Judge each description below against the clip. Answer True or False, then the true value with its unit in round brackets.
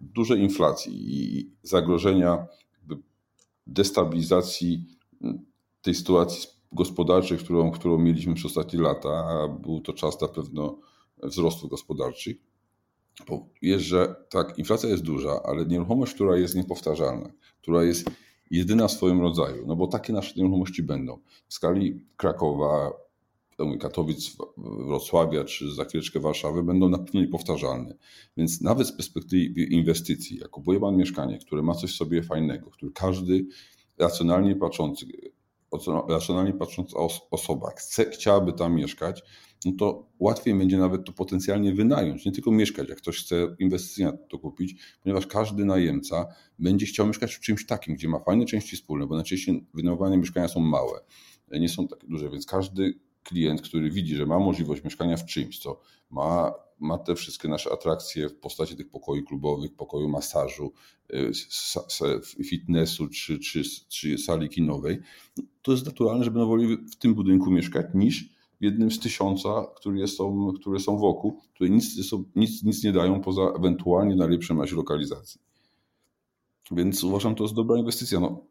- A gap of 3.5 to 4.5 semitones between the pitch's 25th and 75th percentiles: False (2.7 semitones)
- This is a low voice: True (90 Hz)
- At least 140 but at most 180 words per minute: True (150 wpm)